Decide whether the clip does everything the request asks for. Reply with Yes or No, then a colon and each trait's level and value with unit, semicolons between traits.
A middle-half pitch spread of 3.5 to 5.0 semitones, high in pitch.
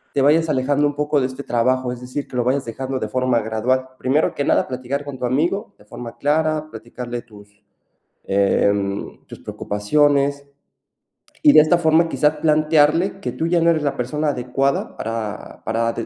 No: average, 4.1 semitones; low, 135 Hz